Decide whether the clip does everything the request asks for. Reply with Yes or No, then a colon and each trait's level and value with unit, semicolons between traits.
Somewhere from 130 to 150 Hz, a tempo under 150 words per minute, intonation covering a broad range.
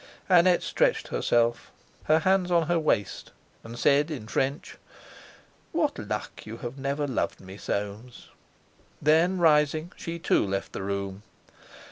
Yes: medium, 140 Hz; average, 140 wpm; wide, 6.9 semitones